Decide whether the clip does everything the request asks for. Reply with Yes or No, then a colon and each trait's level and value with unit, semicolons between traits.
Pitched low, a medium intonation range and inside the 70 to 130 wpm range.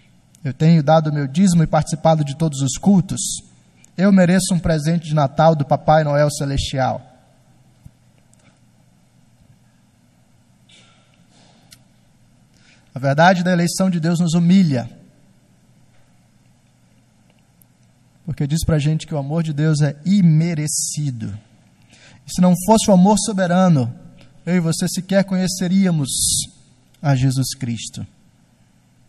No: medium, 155 Hz; average, 4.8 semitones; slow, 120 wpm